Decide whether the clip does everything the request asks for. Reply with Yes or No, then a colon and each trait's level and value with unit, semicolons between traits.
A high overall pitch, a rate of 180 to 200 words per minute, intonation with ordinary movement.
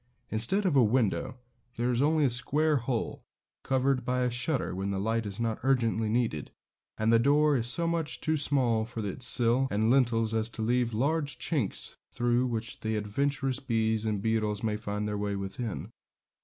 No: low, 120 Hz; average, 185 wpm; average, 3.5 semitones